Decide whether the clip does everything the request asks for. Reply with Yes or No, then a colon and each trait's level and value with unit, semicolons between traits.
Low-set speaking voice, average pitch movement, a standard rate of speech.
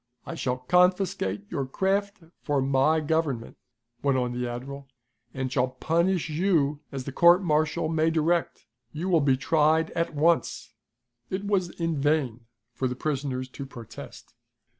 No: medium, 150 Hz; average, 4.2 semitones; average, 150 wpm